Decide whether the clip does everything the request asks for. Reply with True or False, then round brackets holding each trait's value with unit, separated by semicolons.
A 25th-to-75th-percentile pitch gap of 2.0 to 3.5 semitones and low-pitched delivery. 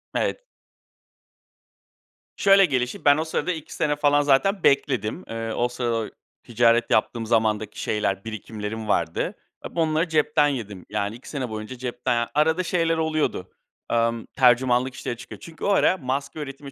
False (5.3 semitones; 125 Hz)